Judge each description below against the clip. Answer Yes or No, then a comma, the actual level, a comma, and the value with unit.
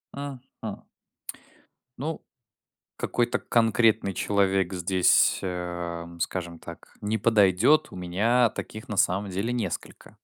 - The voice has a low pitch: Yes, low, 100 Hz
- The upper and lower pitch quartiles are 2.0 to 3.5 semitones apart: No, average, 4.5 semitones